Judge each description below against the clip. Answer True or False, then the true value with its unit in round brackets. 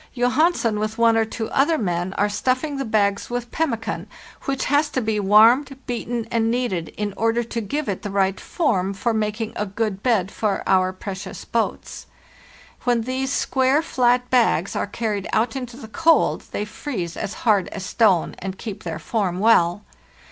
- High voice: True (225 Hz)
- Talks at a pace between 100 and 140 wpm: False (175 wpm)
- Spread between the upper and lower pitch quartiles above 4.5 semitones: False (3.8 semitones)